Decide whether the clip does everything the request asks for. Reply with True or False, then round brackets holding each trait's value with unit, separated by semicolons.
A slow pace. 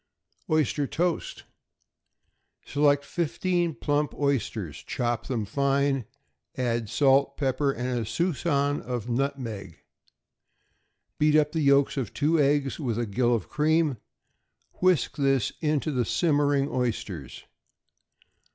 True (115 wpm)